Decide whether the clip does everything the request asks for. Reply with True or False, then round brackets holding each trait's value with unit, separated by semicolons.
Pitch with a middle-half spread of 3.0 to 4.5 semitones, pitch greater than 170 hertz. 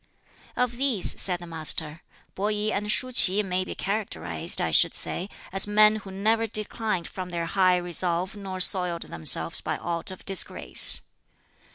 True (3.3 semitones; 190 Hz)